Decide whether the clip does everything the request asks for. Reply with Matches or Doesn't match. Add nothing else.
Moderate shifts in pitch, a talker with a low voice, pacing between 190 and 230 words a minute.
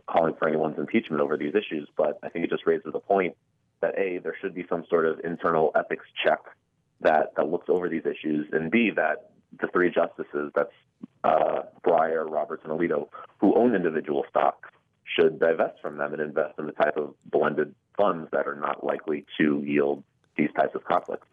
Matches